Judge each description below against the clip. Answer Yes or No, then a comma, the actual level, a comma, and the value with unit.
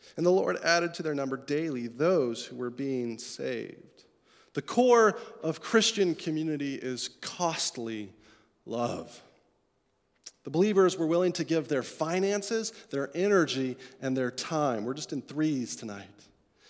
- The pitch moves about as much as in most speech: No, wide, 6.0 semitones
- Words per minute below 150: Yes, average, 140 wpm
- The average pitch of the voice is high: No, medium, 155 Hz